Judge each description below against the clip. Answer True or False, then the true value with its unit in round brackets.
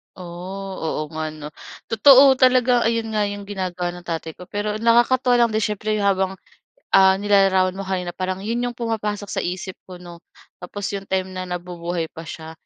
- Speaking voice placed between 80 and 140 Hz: False (195 Hz)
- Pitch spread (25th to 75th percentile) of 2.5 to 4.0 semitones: True (3.4 semitones)